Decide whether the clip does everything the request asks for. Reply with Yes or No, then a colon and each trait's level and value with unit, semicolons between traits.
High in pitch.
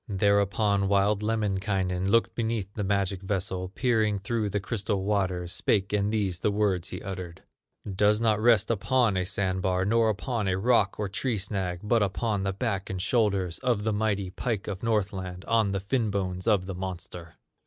No: low, 100 Hz